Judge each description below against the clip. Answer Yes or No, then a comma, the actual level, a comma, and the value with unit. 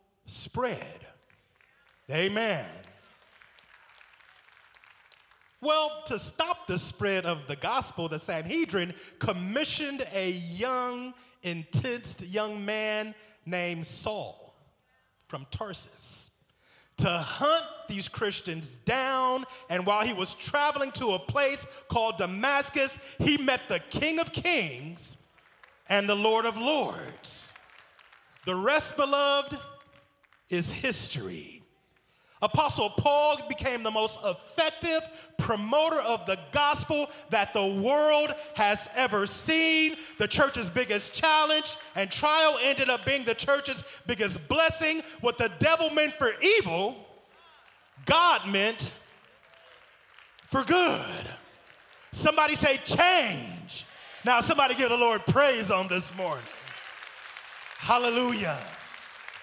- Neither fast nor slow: No, slow, 105 wpm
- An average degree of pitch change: No, wide, 6.8 semitones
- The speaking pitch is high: Yes, very high, 250 Hz